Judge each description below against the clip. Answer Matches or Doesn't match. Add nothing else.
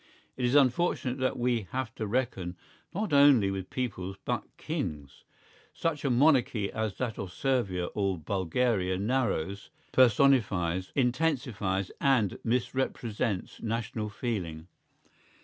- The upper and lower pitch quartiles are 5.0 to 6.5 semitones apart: Matches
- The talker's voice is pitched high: Doesn't match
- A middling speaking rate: Doesn't match